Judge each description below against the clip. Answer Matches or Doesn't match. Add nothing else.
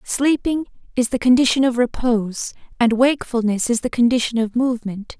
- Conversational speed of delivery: Matches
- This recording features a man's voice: Doesn't match